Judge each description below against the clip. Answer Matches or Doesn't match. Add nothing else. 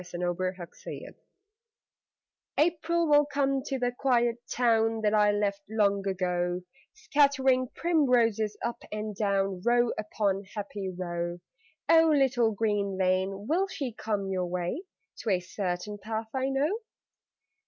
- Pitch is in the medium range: Doesn't match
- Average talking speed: Doesn't match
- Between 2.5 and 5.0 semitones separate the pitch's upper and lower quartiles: Doesn't match